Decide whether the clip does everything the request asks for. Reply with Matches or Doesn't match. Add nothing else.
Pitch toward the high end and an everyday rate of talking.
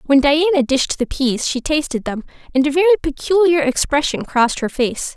Matches